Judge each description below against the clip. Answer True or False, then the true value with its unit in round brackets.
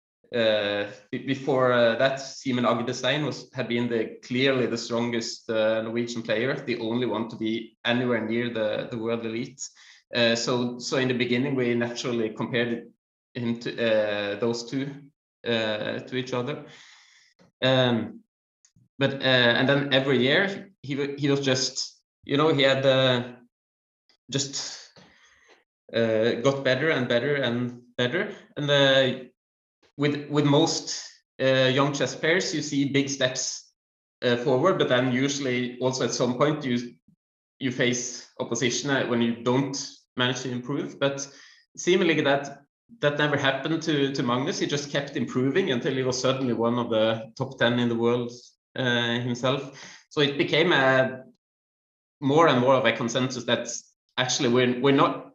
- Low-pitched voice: True (125 Hz)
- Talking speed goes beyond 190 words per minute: False (160 wpm)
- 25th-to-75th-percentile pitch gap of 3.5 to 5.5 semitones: False (2.7 semitones)